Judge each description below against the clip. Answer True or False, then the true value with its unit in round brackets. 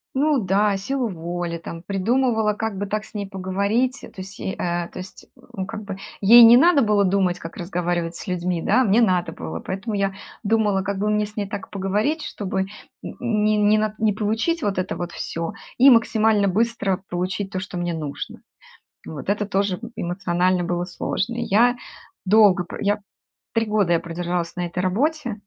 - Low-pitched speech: False (200 Hz)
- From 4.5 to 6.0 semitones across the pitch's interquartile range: False (3.2 semitones)